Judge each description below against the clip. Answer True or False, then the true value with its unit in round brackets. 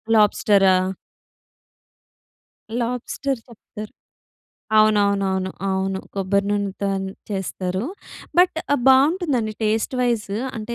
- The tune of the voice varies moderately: True (3.5 semitones)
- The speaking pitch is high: True (210 Hz)